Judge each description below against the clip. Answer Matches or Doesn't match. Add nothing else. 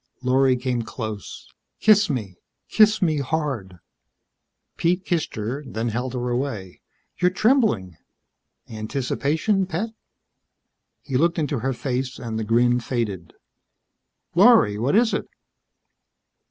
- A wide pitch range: Matches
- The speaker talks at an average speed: Doesn't match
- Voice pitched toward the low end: Matches